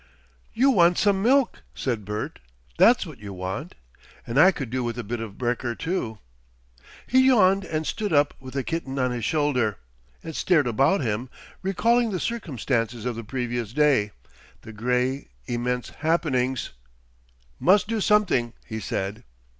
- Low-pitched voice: Yes, low, 130 Hz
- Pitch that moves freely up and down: Yes, wide, 7.5 semitones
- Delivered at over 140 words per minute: Yes, average, 155 wpm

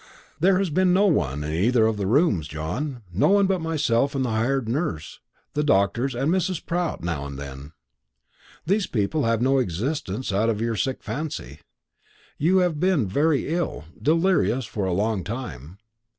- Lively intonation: Yes, wide, 8.5 semitones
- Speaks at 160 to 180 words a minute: Yes, average, 175 wpm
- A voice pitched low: Yes, low, 125 Hz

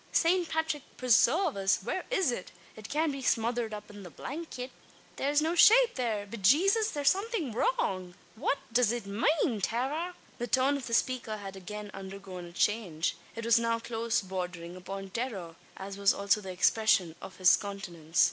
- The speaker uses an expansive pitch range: Yes, wide, 6.3 semitones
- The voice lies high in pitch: Yes, high, 225 Hz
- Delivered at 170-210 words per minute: Yes, average, 175 wpm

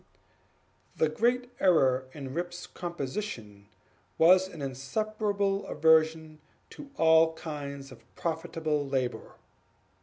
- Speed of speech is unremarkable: No, slow, 95 wpm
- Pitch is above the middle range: No, medium, 160 Hz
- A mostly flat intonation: No, average, 4.8 semitones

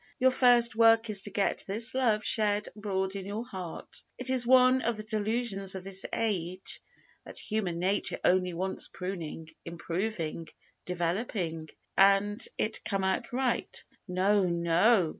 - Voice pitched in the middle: No, high, 200 Hz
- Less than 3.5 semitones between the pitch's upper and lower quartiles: No, average, 3.8 semitones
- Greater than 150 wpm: No, average, 145 wpm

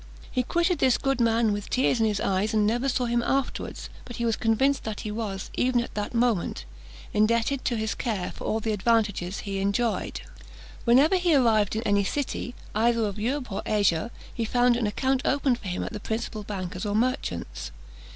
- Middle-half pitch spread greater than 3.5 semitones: No, average, 3.1 semitones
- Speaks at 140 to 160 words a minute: No, average, 200 wpm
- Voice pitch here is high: Yes, high, 225 Hz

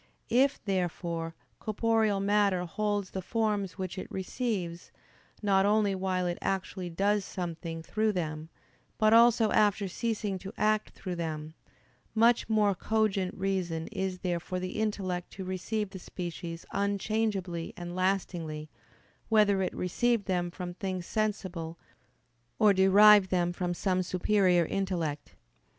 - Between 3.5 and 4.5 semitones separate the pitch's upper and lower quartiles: No, average, 3.0 semitones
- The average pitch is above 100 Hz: Yes, high, 190 Hz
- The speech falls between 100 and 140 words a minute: Yes, slow, 135 wpm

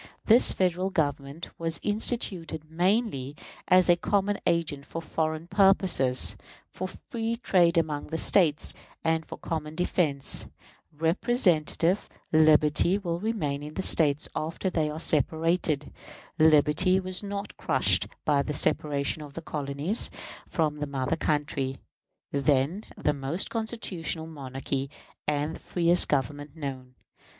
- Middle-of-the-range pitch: Yes, medium, 160 Hz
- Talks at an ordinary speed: No, slow, 125 wpm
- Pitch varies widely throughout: No, average, 3.9 semitones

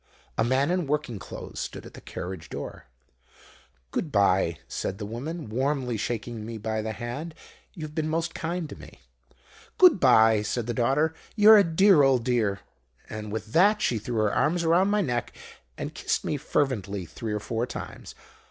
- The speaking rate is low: No, average, 180 wpm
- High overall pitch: No, low, 125 Hz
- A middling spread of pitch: No, wide, 6.6 semitones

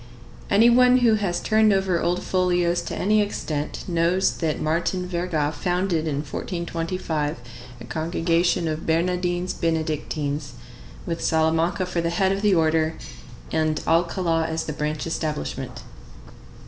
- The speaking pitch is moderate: Yes, medium, 170 Hz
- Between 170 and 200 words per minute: No, slow, 135 wpm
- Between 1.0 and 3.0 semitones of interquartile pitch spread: Yes, narrow, 2.5 semitones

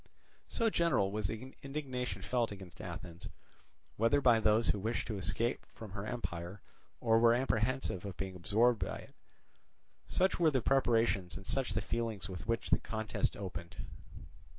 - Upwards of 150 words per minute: Yes, average, 160 wpm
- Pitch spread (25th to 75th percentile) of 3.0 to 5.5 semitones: Yes, average, 4.2 semitones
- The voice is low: Yes, low, 110 Hz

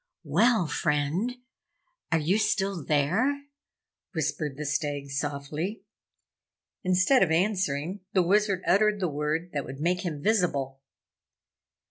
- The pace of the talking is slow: Yes, slow, 115 wpm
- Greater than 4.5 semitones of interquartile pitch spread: Yes, average, 5.2 semitones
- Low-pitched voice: No, medium, 170 Hz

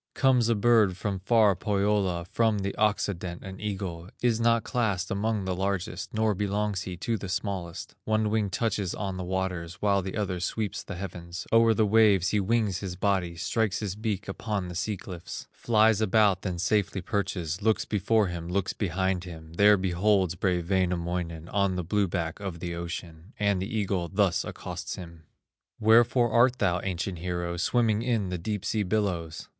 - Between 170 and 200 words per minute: Yes, average, 180 wpm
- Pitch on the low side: Yes, very low, 95 Hz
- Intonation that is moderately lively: Yes, average, 3.1 semitones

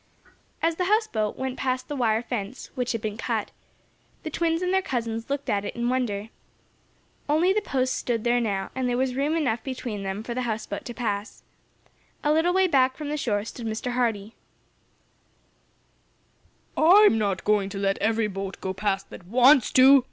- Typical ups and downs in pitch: Yes, average, 4.6 semitones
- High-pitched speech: Yes, high, 245 Hz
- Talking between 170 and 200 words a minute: Yes, average, 185 wpm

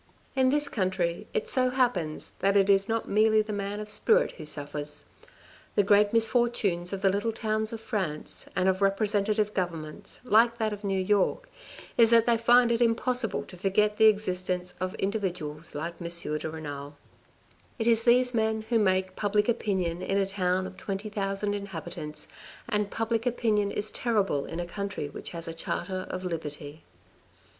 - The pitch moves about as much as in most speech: Yes, average, 3.7 semitones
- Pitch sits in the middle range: No, high, 200 Hz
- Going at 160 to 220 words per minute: Yes, average, 175 wpm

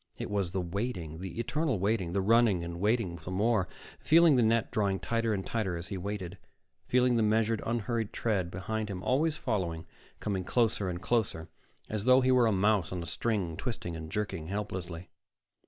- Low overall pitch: Yes, low, 105 Hz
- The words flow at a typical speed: Yes, average, 185 wpm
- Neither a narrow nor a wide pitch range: Yes, average, 4.2 semitones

